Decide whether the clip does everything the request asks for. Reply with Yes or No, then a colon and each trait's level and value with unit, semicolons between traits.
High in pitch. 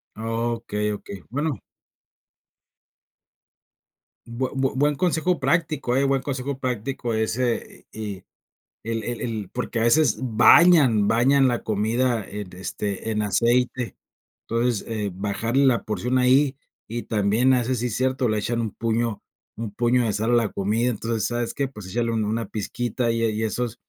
No: low, 115 Hz